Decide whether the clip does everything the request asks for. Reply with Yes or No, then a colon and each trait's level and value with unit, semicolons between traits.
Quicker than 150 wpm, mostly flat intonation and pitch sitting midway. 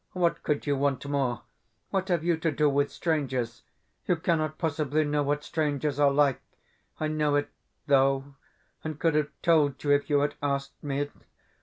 Yes: average, 175 wpm; narrow, 1.8 semitones; medium, 145 Hz